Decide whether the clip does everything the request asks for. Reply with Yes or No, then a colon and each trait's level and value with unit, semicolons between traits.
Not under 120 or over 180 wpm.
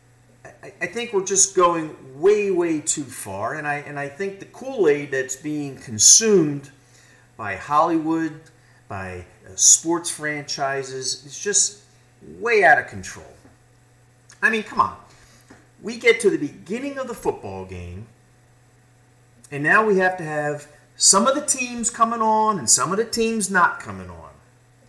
Yes: average, 155 wpm